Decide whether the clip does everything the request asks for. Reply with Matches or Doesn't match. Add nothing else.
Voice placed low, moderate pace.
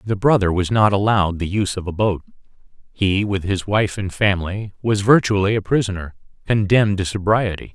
Matches